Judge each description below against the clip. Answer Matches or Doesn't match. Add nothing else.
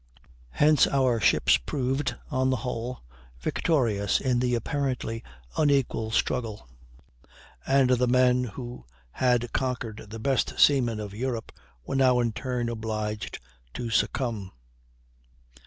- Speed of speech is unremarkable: Doesn't match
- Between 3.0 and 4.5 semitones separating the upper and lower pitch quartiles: Doesn't match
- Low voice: Matches